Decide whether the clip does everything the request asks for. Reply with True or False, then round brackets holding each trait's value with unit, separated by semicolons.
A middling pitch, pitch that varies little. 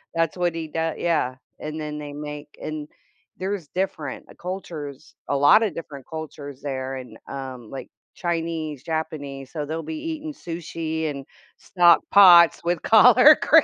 False (160 Hz; 3.4 semitones)